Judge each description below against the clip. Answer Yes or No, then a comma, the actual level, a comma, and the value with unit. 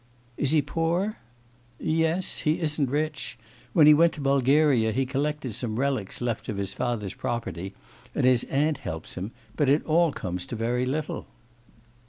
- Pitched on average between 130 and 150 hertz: Yes, low, 135 Hz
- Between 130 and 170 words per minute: Yes, average, 165 wpm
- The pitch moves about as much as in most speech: Yes, average, 4.6 semitones